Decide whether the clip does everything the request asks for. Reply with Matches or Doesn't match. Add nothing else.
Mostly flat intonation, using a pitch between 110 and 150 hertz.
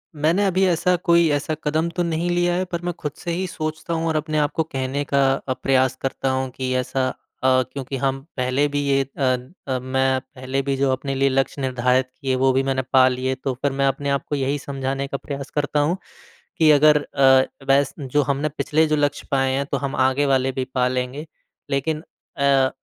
Matches